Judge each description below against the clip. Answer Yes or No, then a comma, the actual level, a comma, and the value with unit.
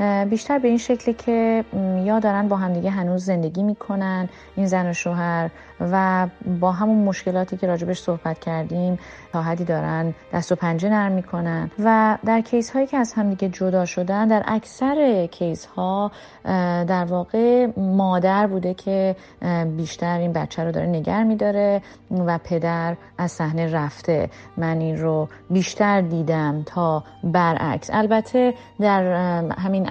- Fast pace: No, average, 145 wpm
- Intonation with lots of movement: No, average, 3.3 semitones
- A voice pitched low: No, medium, 185 Hz